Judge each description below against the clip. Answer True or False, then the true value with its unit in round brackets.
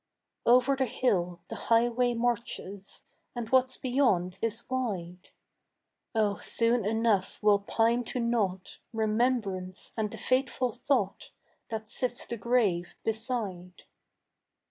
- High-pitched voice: True (225 Hz)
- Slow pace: True (115 wpm)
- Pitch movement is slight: False (3.7 semitones)